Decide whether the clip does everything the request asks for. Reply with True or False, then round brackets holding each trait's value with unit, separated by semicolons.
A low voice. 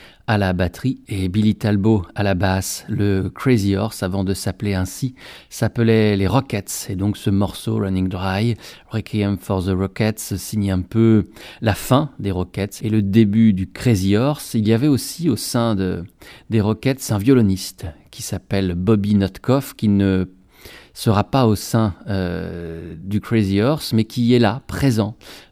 True (105 Hz)